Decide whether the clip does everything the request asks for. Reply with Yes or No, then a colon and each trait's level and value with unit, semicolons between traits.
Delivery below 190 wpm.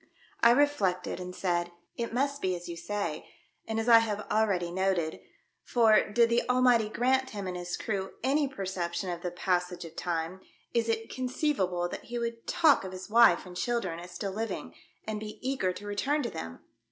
No: average, 195 wpm